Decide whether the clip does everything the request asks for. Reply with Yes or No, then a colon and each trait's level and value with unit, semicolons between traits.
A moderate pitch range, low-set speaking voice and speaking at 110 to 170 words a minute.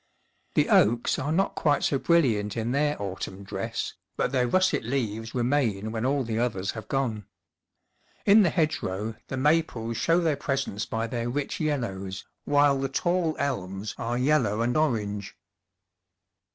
Yes: average, 4.9 semitones; low, 125 Hz; average, 150 wpm